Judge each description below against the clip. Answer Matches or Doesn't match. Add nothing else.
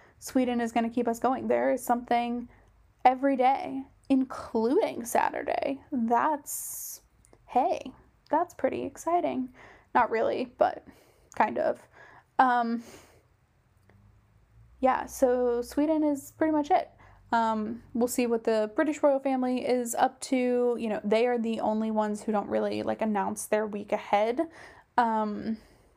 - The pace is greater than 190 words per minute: Doesn't match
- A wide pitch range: Doesn't match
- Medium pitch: Doesn't match